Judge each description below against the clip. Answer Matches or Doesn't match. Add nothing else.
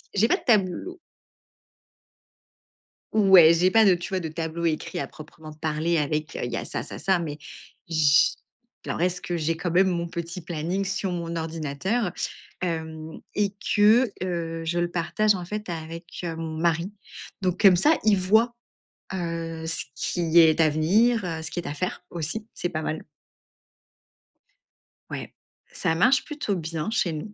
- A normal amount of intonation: Matches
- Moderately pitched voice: Matches